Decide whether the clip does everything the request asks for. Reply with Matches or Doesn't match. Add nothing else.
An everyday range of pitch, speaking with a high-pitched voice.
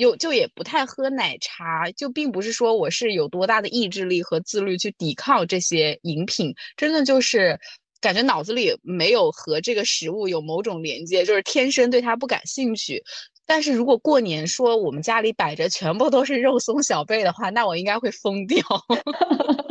Doesn't match